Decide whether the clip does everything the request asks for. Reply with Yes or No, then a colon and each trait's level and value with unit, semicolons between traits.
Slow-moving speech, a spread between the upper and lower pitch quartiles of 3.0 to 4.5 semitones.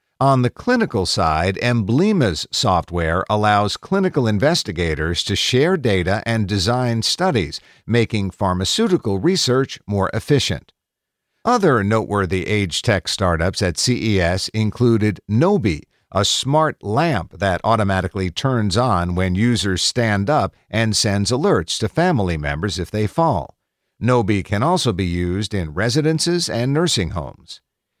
No: slow, 125 wpm; average, 4.9 semitones